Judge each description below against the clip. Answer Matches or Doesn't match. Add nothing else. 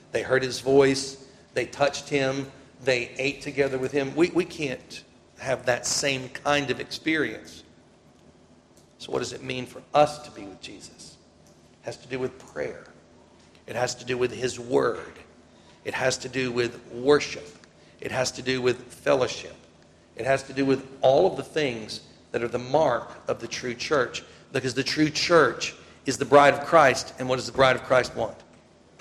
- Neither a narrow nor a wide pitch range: Doesn't match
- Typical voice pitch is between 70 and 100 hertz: Doesn't match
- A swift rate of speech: Doesn't match